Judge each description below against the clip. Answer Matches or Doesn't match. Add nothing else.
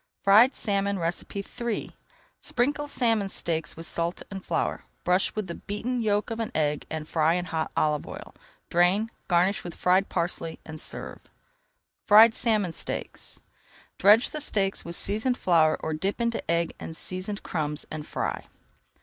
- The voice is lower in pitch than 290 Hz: Matches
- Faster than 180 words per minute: Doesn't match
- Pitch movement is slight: Doesn't match